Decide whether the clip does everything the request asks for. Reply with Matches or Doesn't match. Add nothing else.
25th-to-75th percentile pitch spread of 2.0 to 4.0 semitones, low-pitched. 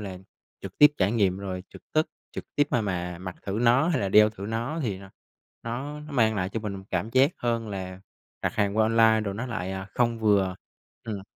Matches